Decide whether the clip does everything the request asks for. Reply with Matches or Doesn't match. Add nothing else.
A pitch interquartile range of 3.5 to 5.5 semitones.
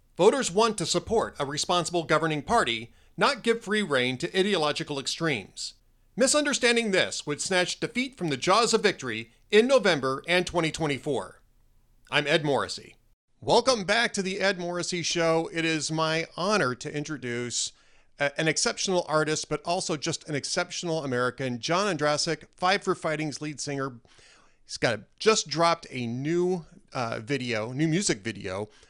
Matches